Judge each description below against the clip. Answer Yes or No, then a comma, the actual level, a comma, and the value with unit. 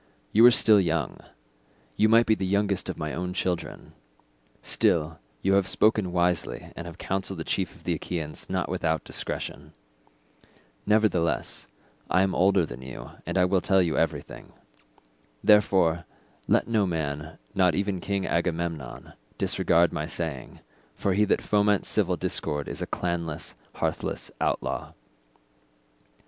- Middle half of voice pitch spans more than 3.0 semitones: Yes, average, 3.6 semitones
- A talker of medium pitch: No, very low, 90 Hz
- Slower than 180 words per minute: Yes, average, 140 wpm